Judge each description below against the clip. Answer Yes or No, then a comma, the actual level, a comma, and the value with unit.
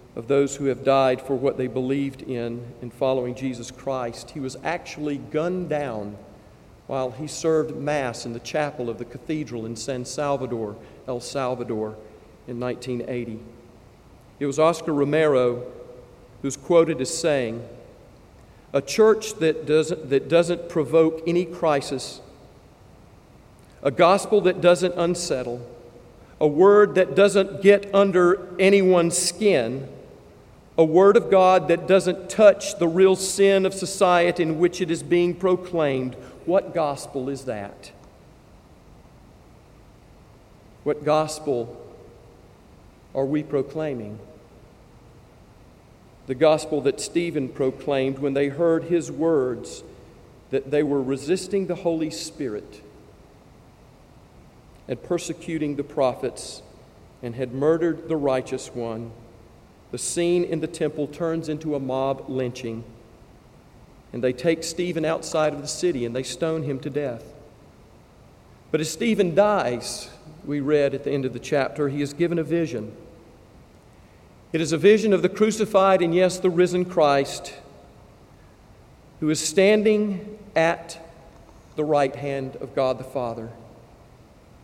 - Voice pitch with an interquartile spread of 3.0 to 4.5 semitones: No, average, 5.2 semitones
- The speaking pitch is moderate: Yes, medium, 145 Hz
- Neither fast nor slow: No, slow, 130 wpm